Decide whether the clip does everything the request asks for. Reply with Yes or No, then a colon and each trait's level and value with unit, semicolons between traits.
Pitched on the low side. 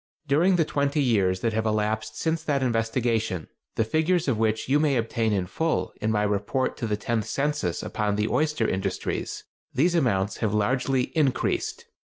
Yes: low, 115 Hz